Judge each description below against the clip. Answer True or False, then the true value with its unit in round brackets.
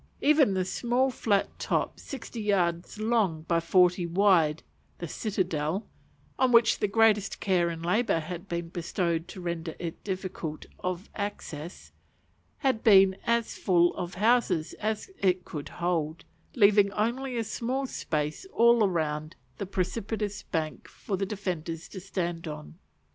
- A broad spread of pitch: False (4.2 semitones)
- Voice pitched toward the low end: False (185 Hz)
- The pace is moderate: True (145 wpm)